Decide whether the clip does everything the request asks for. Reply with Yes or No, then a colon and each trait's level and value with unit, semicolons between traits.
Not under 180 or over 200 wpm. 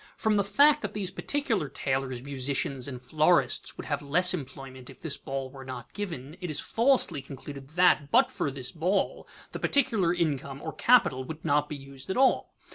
Yes: average, 190 wpm